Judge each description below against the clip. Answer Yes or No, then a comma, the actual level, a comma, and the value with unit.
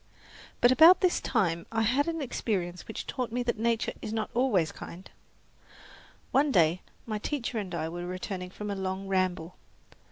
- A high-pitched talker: Yes, high, 210 Hz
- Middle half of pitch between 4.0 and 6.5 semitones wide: Yes, average, 5.2 semitones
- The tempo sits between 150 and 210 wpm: Yes, average, 170 wpm